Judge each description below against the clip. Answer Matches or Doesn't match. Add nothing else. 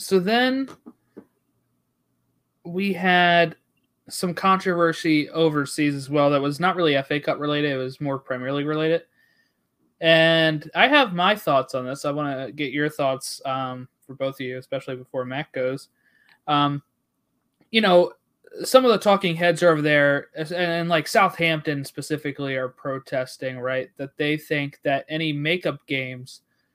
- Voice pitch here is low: Doesn't match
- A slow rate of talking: Doesn't match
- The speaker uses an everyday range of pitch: Matches